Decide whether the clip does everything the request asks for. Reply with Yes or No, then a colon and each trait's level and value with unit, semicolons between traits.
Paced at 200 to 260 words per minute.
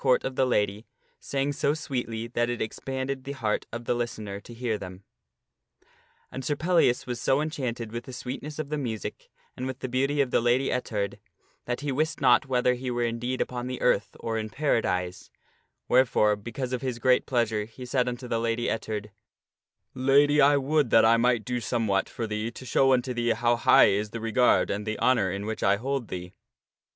Yes: fast, 205 wpm